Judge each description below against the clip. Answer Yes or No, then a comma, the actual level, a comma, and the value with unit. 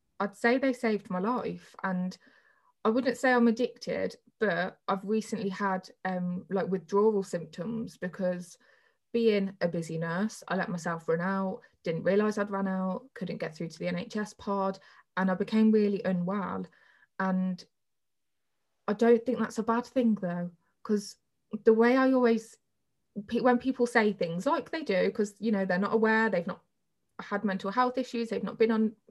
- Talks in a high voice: Yes, high, 205 Hz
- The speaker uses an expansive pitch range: No, average, 3.7 semitones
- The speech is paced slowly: No, average, 175 wpm